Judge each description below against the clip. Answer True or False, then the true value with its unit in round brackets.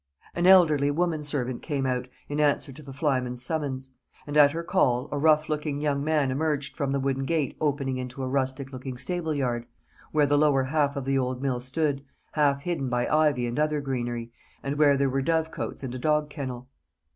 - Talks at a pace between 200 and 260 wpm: True (205 wpm)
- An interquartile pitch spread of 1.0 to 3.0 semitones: True (2.5 semitones)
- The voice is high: False (140 Hz)